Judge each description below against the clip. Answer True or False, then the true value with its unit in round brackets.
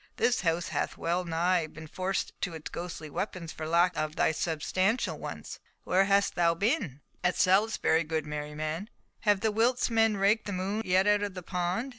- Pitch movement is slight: False (4.0 semitones)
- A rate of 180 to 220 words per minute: True (185 wpm)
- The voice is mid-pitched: True (180 Hz)